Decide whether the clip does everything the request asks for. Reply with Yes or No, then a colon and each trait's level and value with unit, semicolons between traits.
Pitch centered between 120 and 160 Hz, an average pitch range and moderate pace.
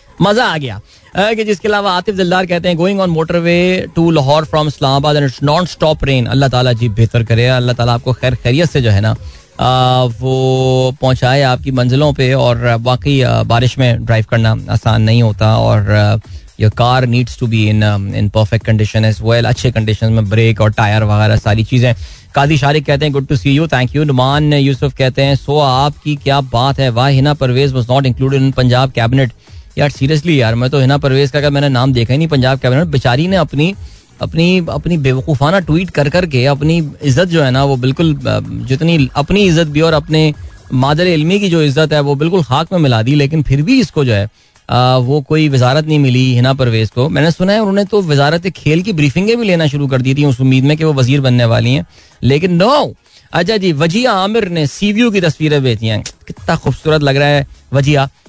No: low, 135 Hz; average, 4.1 semitones; fast, 210 wpm